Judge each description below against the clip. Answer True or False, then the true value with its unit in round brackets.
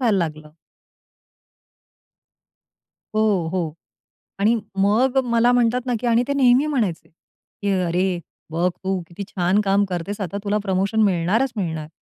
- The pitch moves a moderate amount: True (4.7 semitones)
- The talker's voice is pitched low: False (200 Hz)